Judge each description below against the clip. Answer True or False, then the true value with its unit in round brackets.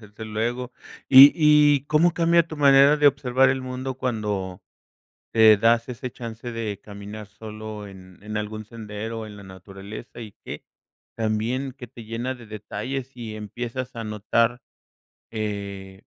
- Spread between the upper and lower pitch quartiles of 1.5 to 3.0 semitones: False (3.5 semitones)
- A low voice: True (115 Hz)